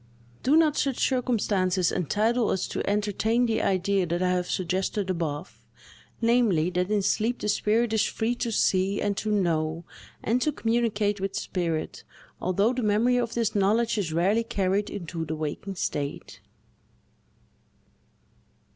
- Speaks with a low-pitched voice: No, high, 205 Hz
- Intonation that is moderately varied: Yes, average, 3.9 semitones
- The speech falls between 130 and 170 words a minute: Yes, average, 145 wpm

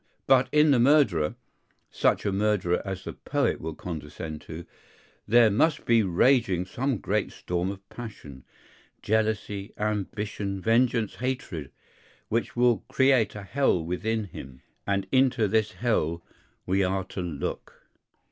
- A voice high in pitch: No, low, 105 Hz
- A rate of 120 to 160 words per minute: Yes, slow, 135 wpm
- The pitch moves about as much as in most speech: Yes, average, 4.8 semitones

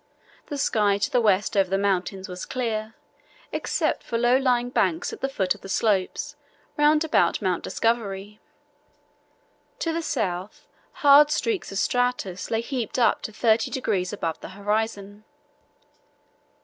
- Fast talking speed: No, average, 150 wpm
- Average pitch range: Yes, average, 4.6 semitones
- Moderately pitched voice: No, high, 220 Hz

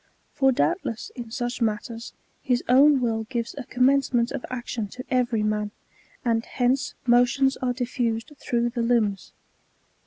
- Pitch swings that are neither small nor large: No, narrow, 1.9 semitones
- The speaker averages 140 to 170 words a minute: Yes, average, 150 wpm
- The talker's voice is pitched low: No, high, 240 Hz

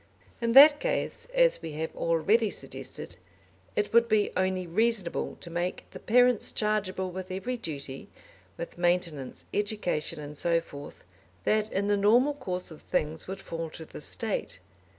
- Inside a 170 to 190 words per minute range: No, average, 155 wpm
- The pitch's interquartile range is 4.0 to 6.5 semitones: Yes, average, 4.8 semitones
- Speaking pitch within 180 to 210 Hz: Yes, medium, 185 Hz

